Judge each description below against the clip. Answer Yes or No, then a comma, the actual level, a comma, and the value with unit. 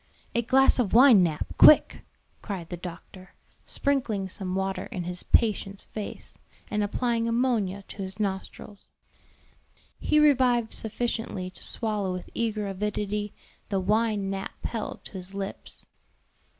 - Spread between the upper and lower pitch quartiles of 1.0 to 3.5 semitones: Yes, average, 3.2 semitones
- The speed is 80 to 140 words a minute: Yes, slow, 135 wpm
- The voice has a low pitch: No, high, 205 Hz